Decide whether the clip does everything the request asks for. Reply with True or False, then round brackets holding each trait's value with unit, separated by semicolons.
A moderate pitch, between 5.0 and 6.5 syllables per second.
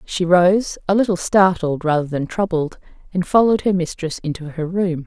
True (175 Hz; 5.1 syllables/s)